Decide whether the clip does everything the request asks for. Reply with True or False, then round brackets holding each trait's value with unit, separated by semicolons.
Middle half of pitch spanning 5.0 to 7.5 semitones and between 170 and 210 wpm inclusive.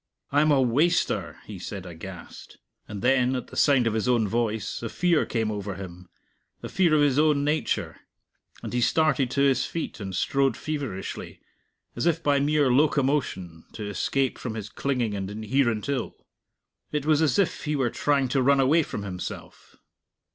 True (5.4 semitones; 175 wpm)